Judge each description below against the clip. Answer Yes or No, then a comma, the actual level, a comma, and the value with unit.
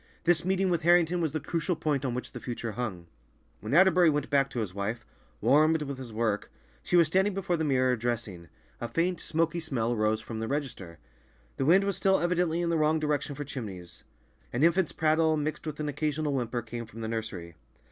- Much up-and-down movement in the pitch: Yes, wide, 6.1 semitones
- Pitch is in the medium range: Yes, medium, 145 Hz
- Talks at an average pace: No, fast, 210 wpm